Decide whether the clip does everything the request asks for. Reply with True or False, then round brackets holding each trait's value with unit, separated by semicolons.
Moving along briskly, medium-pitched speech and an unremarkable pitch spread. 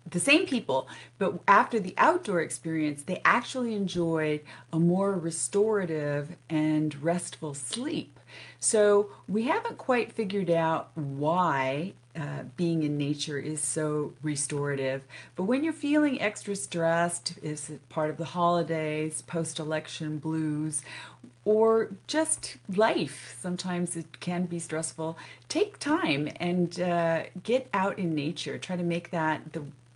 False (135 wpm; 165 Hz; 4.5 semitones)